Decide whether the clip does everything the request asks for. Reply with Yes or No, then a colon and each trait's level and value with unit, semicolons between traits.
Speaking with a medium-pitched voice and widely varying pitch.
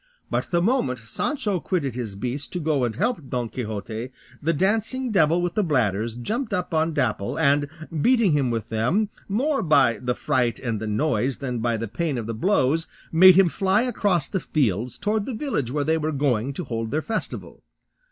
Yes: medium, 145 Hz; wide, 7.9 semitones